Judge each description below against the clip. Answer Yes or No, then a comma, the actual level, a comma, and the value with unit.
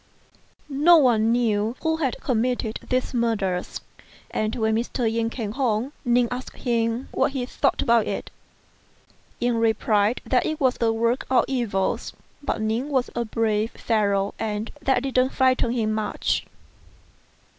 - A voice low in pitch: No, high, 235 Hz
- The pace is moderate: Yes, average, 145 wpm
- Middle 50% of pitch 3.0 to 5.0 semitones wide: No, narrow, 2.6 semitones